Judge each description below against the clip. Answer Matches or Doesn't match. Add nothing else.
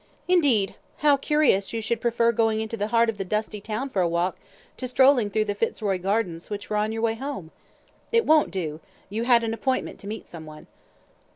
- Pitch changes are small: Doesn't match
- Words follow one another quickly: Matches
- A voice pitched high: Matches